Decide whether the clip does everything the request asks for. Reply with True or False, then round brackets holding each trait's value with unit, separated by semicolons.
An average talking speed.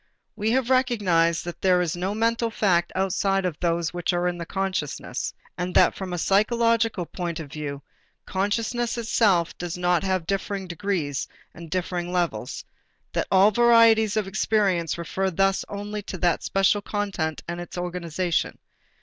True (155 wpm)